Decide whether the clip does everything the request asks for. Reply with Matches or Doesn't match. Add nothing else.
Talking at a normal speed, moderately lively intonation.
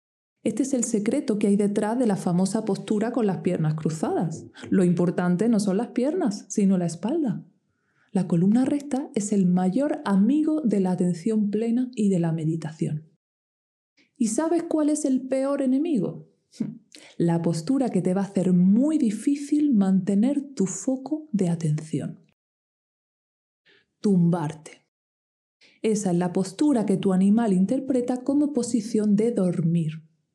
Doesn't match